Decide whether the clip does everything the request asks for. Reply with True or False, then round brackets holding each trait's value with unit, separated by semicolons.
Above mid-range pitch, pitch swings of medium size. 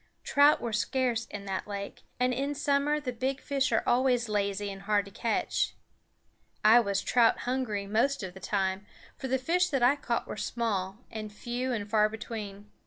True (230 Hz; 4.2 semitones)